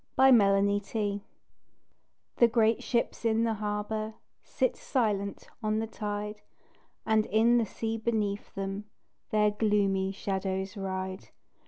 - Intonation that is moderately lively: No, narrow, 2.0 semitones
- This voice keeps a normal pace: No, slow, 120 wpm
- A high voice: Yes, high, 210 Hz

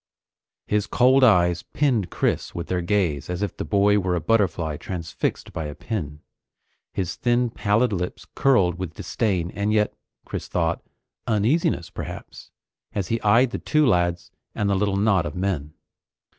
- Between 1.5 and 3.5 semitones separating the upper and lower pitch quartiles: No, average, 4.0 semitones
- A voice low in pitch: Yes, low, 100 Hz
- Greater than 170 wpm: No, average, 160 wpm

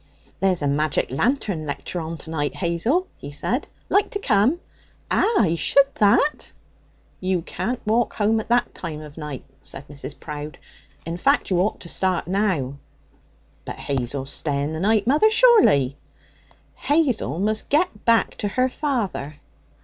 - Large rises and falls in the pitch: Yes, wide, 8.2 semitones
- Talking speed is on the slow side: No, average, 150 wpm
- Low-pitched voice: No, medium, 185 Hz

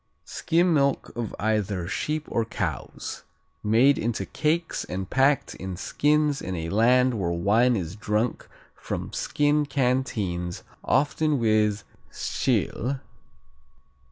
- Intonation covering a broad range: Yes, wide, 5.8 semitones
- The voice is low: Yes, low, 120 Hz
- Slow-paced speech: Yes, slow, 115 wpm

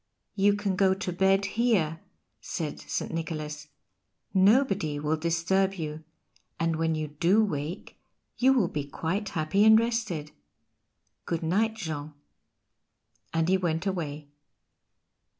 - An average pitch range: Yes, average, 4.2 semitones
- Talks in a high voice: No, medium, 170 Hz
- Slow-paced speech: Yes, slow, 125 wpm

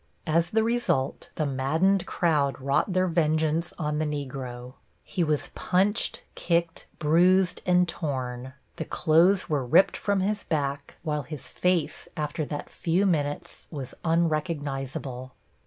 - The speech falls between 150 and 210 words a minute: No, slow, 135 wpm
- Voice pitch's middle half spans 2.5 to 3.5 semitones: No, average, 4.1 semitones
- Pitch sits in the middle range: Yes, medium, 155 Hz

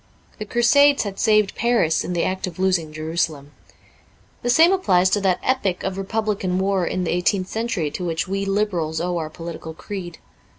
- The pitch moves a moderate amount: Yes, average, 3.8 semitones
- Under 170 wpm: No, average, 185 wpm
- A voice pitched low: No, high, 190 Hz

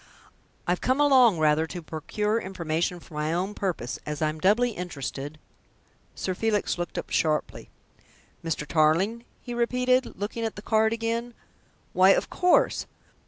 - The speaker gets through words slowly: No, average, 155 wpm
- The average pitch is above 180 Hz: Yes, high, 190 Hz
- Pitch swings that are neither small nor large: No, wide, 6.4 semitones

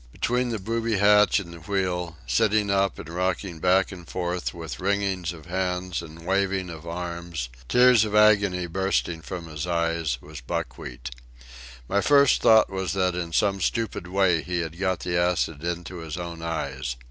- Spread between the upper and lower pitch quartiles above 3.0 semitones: No, average, 2.7 semitones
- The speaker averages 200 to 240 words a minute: No, average, 170 wpm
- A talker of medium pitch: No, very low, 90 Hz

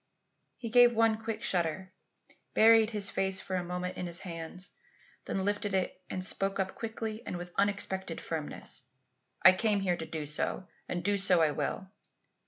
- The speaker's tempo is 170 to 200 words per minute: Yes, average, 175 wpm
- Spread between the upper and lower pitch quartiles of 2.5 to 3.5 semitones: Yes, average, 2.9 semitones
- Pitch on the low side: No, high, 190 Hz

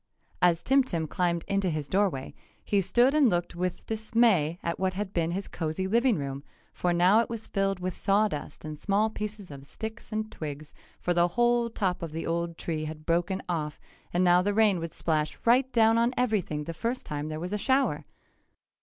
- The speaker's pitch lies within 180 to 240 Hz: Yes, medium, 185 Hz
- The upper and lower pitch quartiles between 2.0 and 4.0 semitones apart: No, average, 4.8 semitones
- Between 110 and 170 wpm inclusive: No, average, 200 wpm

